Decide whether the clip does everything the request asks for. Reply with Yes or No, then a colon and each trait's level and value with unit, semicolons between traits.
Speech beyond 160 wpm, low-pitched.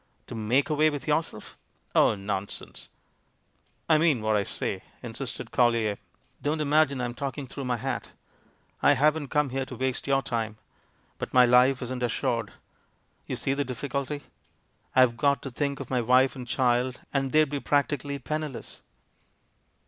Yes: average, 170 wpm; low, 130 Hz